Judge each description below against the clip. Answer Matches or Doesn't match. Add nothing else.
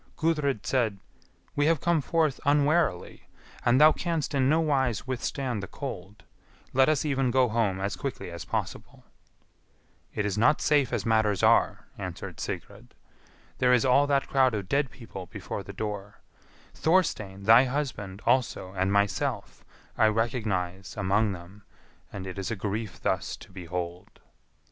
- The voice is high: Doesn't match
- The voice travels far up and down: Matches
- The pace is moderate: Matches